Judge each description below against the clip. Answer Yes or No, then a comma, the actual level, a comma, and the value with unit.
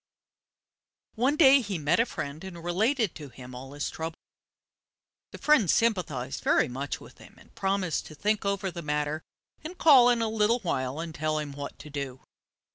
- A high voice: No, medium, 170 Hz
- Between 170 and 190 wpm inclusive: Yes, average, 185 wpm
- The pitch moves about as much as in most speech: No, wide, 7.2 semitones